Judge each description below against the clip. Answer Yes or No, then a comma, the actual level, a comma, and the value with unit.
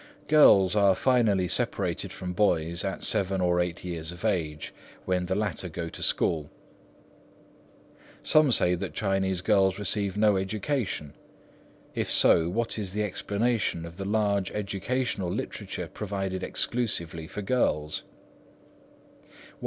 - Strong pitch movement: No, average, 3.1 semitones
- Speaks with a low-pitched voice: Yes, very low, 95 Hz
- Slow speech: Yes, slow, 130 wpm